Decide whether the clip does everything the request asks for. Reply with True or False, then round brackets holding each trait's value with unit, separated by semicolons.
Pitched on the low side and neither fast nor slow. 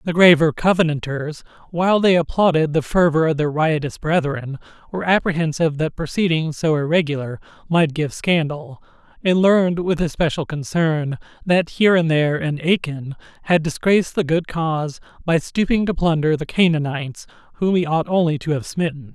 False (160 Hz; 155 wpm)